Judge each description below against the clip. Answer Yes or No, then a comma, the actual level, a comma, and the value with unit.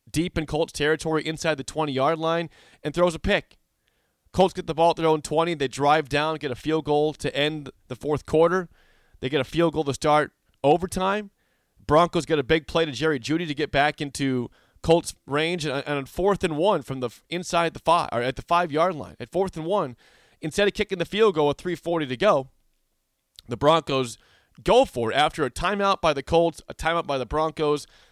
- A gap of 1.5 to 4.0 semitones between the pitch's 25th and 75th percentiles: Yes, average, 2.9 semitones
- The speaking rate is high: Yes, fast, 210 wpm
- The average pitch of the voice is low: No, medium, 155 Hz